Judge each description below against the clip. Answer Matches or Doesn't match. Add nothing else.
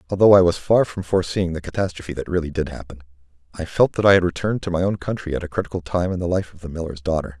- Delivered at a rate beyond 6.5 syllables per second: Matches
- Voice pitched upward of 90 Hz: Doesn't match